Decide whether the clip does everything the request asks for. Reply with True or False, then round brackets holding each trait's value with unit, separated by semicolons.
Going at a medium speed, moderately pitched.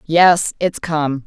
True (145 wpm; 160 Hz)